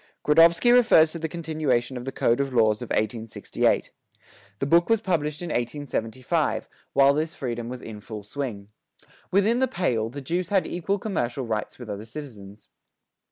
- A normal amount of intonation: No, wide, 6.5 semitones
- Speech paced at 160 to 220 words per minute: Yes, average, 165 wpm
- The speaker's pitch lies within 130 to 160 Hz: Yes, low, 135 Hz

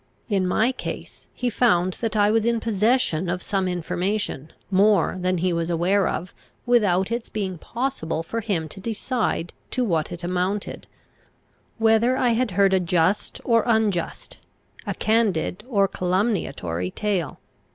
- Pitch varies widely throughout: No, average, 4.2 semitones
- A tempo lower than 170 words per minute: Yes, average, 150 wpm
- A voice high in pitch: Yes, high, 195 Hz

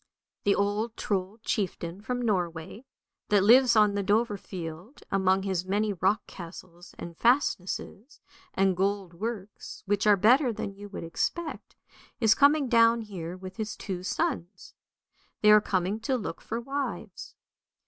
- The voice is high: Yes, high, 205 Hz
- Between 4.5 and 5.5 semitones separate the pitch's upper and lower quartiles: No, average, 3.5 semitones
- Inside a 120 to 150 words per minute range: Yes, average, 145 wpm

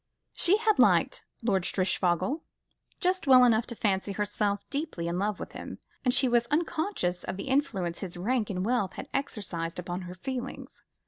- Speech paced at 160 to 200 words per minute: Yes, average, 175 wpm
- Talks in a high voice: Yes, high, 210 Hz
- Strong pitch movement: Yes, wide, 6.4 semitones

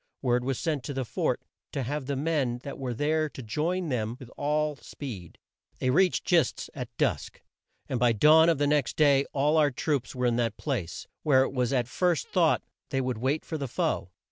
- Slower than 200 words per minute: No, fast, 205 wpm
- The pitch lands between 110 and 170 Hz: Yes, low, 135 Hz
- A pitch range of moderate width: Yes, average, 3.6 semitones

